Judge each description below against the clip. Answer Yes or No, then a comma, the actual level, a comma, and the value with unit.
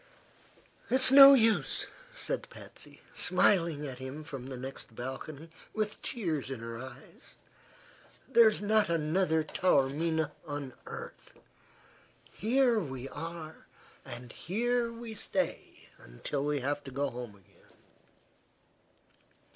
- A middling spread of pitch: No, wide, 8.0 semitones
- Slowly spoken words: Yes, slow, 115 wpm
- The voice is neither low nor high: Yes, medium, 155 Hz